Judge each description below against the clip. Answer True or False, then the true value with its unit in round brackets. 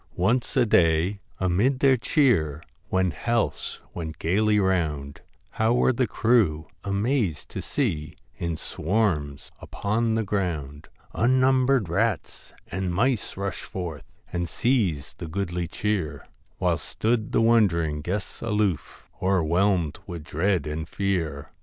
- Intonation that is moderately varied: False (5.7 semitones)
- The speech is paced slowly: True (130 wpm)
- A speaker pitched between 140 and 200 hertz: False (95 Hz)